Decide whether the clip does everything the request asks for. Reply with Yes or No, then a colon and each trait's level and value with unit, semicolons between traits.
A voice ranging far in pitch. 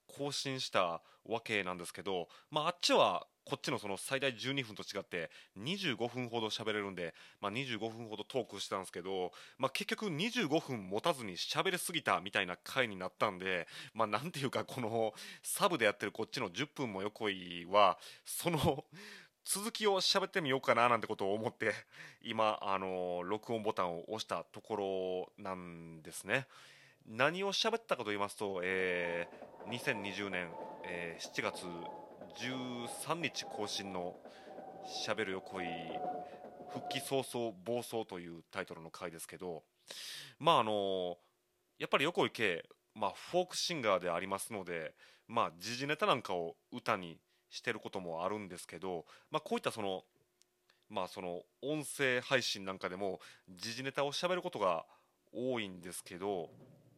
Yes: wide, 6.3 semitones